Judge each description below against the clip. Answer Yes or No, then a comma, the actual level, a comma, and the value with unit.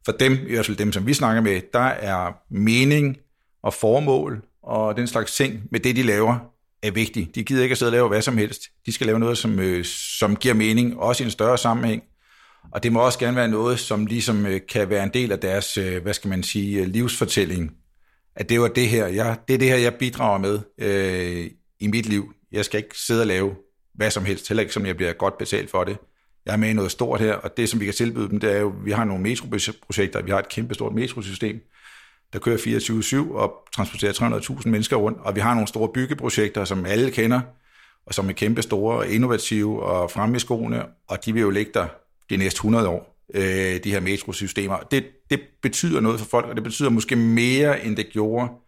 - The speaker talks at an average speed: No, fast, 230 wpm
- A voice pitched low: Yes, low, 110 Hz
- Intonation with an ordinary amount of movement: Yes, average, 3.0 semitones